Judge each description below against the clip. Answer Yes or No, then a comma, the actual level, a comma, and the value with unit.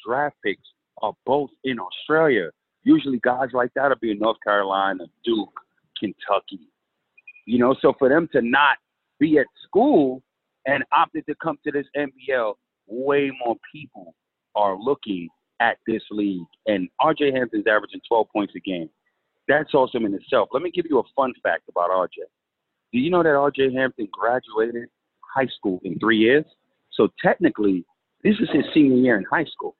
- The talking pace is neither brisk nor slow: Yes, average, 170 wpm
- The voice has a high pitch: No, low, 135 Hz